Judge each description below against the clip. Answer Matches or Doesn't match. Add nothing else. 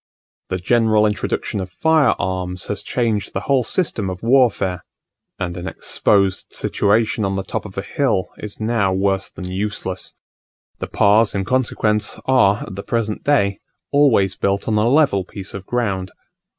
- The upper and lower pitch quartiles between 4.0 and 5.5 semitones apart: Doesn't match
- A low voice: Matches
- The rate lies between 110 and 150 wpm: Doesn't match